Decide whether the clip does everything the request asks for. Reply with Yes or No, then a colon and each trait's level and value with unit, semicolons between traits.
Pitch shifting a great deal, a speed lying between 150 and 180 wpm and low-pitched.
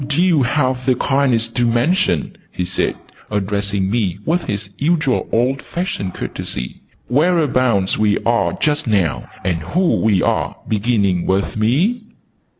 No: wide, 6.6 semitones; average, 140 wpm; low, 120 Hz